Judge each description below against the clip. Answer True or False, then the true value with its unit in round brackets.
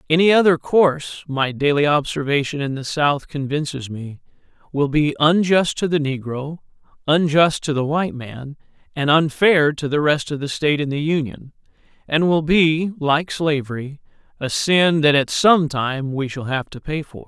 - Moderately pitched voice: True (150 Hz)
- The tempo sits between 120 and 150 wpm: False (175 wpm)